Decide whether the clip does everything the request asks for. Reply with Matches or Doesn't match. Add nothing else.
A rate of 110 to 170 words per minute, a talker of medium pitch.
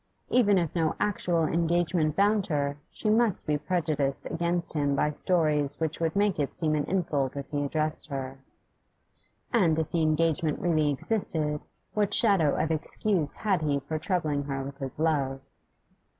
Matches